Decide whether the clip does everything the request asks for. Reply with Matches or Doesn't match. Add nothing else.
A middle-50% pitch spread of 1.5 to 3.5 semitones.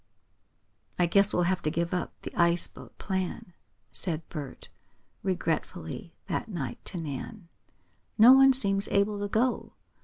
Matches